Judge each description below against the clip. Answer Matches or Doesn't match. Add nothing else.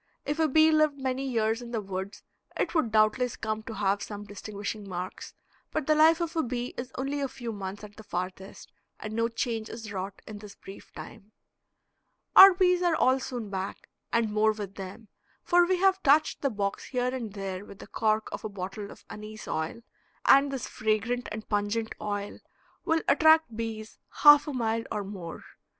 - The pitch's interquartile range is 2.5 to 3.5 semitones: Doesn't match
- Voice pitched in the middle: Doesn't match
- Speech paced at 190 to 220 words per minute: Matches